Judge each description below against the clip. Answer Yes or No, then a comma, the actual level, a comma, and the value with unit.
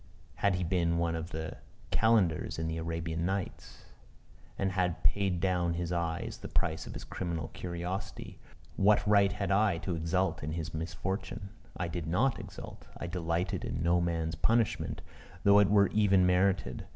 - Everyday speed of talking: Yes, average, 170 wpm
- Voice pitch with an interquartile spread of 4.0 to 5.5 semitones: No, average, 2.8 semitones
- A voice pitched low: Yes, very low, 90 Hz